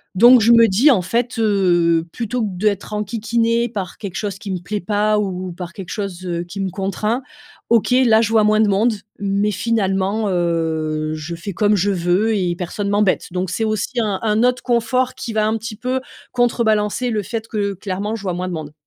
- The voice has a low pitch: No, high, 205 Hz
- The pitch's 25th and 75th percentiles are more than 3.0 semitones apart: Yes, average, 3.4 semitones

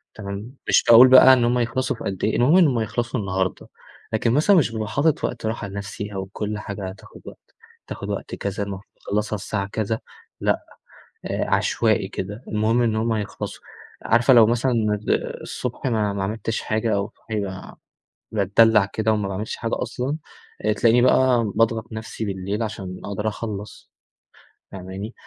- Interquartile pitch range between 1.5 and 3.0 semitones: Yes, average, 2.7 semitones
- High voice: No, low, 110 Hz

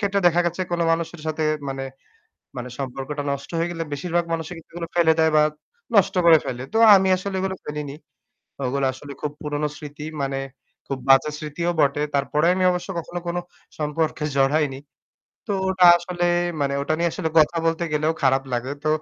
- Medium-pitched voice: Yes, medium, 155 Hz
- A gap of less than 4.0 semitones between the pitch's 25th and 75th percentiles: Yes, average, 3.6 semitones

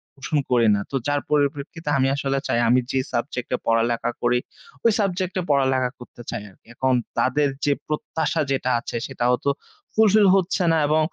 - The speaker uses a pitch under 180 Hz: Yes, low, 135 Hz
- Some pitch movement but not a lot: Yes, average, 3.8 semitones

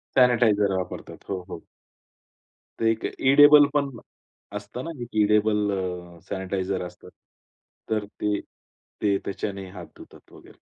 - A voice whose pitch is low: Yes, low, 105 Hz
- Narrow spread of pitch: No, average, 3.0 semitones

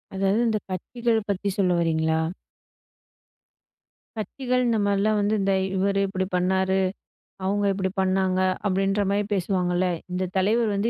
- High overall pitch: Yes, high, 195 Hz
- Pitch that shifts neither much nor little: No, narrow, 1.7 semitones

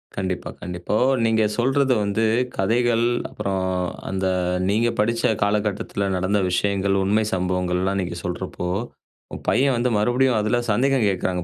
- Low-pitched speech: Yes, low, 100 Hz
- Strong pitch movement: No, average, 3.9 semitones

